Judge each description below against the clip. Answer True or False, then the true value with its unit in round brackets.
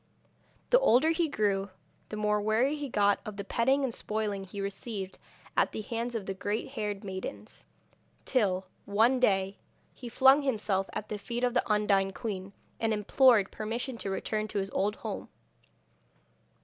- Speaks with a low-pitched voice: False (215 Hz)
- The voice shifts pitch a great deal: False (3.4 semitones)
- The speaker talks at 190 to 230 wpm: False (165 wpm)